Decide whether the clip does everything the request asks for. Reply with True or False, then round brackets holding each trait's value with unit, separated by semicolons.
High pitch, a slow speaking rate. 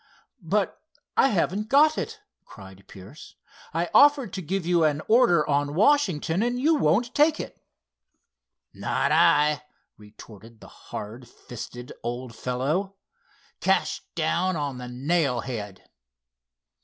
False (155 Hz; 125 wpm)